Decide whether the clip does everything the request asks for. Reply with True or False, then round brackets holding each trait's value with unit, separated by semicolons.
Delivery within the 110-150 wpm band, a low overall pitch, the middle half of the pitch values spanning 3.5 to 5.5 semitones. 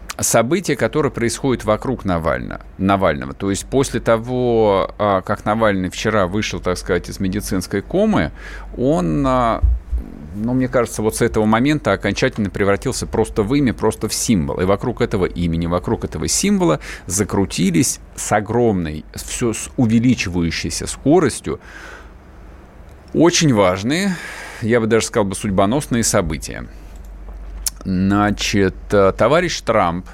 True (120 wpm; 100 Hz; 4.7 semitones)